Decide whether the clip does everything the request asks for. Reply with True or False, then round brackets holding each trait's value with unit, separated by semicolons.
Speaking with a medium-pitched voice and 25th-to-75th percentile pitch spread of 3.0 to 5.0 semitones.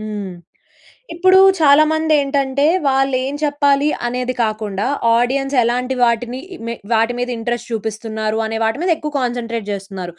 False (245 Hz; 4.0 semitones)